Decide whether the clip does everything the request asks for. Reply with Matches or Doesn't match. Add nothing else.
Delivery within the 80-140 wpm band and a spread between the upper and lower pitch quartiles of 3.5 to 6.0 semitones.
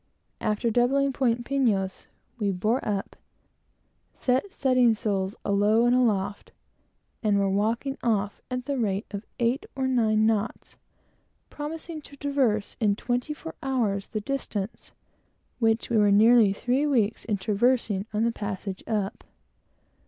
Matches